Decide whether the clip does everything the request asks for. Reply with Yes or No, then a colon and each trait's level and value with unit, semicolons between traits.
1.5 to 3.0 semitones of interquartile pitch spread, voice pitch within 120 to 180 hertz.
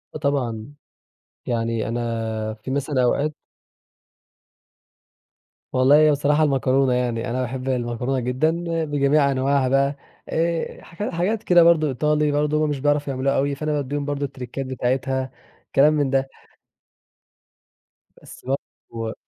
Yes: average, 2.7 semitones; low, 135 Hz